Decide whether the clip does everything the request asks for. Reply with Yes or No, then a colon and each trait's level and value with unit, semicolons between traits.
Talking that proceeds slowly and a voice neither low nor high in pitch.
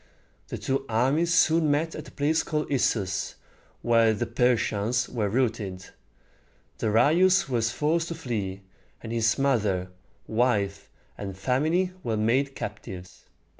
No: slow, 130 wpm; low, 120 Hz